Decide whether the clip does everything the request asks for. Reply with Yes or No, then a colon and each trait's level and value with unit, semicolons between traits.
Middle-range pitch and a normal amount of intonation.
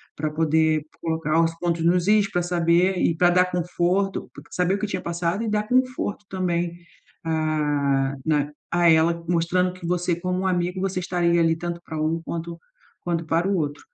No: medium, 170 Hz; narrow, 2.0 semitones